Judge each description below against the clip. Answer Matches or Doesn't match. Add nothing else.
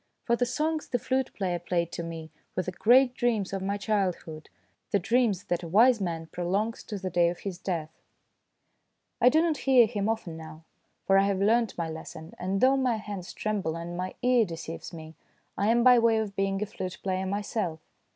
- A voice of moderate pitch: Doesn't match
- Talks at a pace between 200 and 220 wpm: Matches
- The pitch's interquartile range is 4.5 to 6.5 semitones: Matches